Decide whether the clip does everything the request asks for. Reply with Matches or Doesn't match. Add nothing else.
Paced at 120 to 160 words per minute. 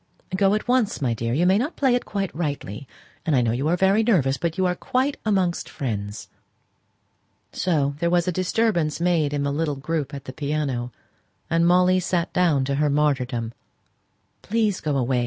Doesn't match